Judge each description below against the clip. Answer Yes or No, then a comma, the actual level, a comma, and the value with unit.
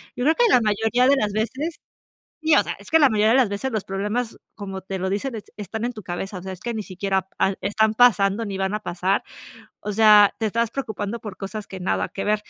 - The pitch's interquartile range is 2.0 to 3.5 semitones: Yes, average, 3.0 semitones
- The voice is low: No, high, 210 Hz